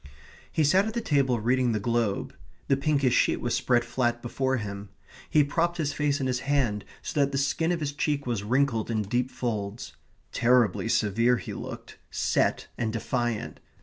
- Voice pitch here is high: No, low, 125 Hz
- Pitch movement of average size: Yes, average, 3.7 semitones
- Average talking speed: Yes, average, 180 wpm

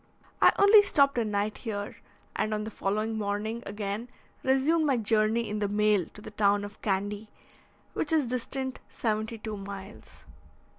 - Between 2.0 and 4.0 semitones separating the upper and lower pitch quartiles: Yes, average, 2.7 semitones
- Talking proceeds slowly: No, average, 160 wpm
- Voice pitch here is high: Yes, high, 215 Hz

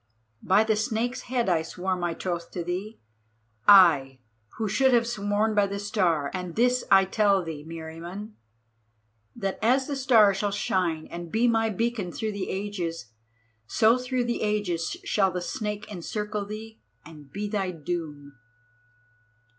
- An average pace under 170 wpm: Yes, average, 155 wpm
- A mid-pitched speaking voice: No, high, 200 Hz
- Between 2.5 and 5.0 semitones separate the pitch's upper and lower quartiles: Yes, average, 4.1 semitones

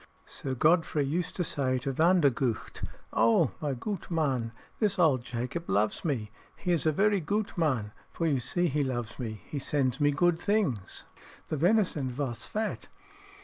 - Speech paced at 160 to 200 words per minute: Yes, average, 165 wpm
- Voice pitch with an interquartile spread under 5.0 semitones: No, wide, 5.5 semitones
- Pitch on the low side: No, medium, 145 Hz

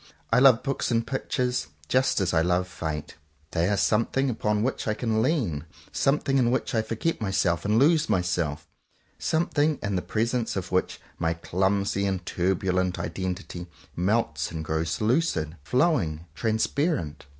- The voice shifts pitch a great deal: Yes, wide, 6.1 semitones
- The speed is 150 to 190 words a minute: Yes, average, 155 wpm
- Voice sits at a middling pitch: No, low, 100 Hz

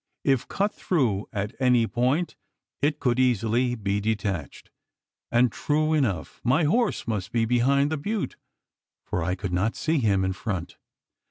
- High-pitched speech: No, low, 120 Hz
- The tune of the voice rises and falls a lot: Yes, wide, 5.8 semitones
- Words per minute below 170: Yes, average, 155 wpm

